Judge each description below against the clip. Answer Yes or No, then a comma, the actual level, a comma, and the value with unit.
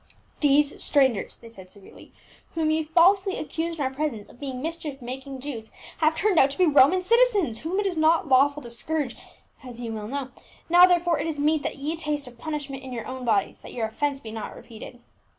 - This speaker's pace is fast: Yes, fast, 215 wpm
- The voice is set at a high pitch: Yes, very high, 285 Hz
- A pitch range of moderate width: Yes, average, 4.4 semitones